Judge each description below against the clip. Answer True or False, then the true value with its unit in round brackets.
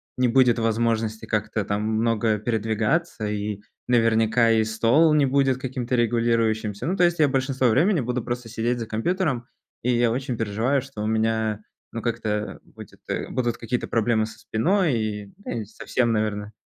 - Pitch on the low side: True (115 Hz)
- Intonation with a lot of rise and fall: False (2.6 semitones)